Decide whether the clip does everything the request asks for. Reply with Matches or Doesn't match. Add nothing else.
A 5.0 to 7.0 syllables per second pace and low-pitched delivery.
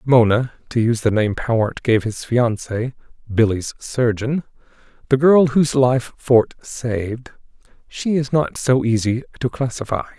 Doesn't match